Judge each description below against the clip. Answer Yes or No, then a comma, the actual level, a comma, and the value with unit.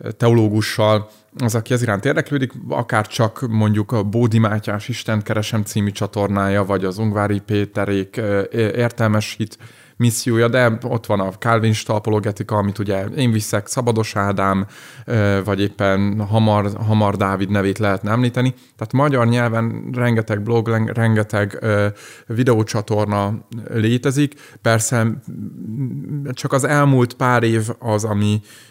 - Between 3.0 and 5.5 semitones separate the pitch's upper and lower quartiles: No, narrow, 2.4 semitones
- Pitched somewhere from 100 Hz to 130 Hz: Yes, low, 110 Hz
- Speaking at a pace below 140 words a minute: Yes, average, 125 wpm